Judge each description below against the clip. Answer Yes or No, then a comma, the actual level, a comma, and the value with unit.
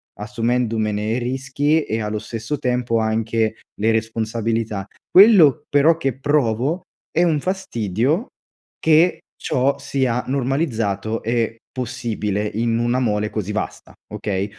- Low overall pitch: Yes, low, 115 Hz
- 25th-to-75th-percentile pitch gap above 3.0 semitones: Yes, average, 3.8 semitones